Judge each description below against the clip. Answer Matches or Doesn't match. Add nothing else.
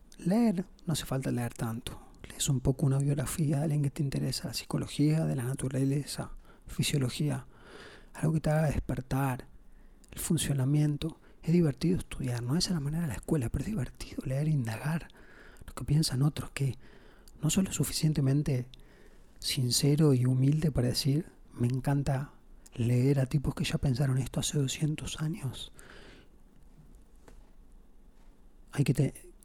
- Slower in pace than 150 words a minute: Doesn't match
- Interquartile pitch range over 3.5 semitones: Doesn't match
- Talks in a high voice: Doesn't match